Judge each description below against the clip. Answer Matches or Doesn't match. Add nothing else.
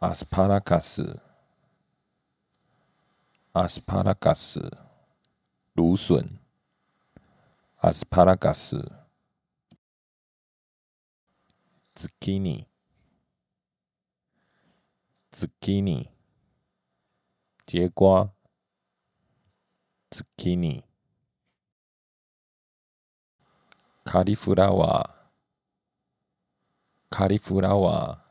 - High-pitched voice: Doesn't match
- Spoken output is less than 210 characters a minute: Matches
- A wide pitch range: Doesn't match